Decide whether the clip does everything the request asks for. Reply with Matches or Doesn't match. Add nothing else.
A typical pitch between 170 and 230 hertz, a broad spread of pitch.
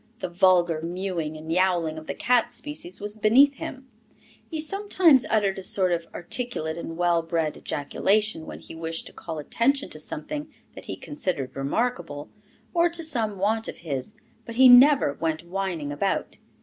Matches